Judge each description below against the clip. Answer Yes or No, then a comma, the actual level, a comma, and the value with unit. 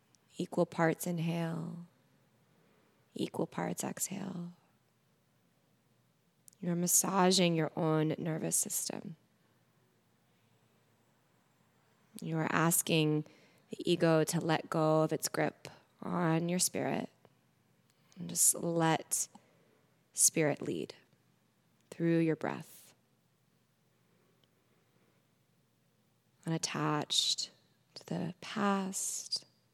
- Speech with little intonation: Yes, narrow, 1.9 semitones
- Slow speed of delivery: Yes, slow, 75 wpm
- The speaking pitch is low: No, medium, 165 Hz